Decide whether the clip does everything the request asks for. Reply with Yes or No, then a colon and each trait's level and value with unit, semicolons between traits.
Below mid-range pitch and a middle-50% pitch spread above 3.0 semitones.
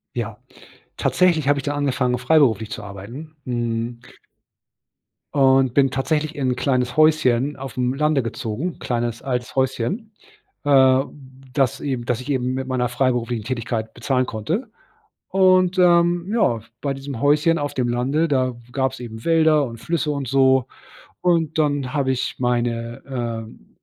Yes: low, 130 Hz; average, 3.7 semitones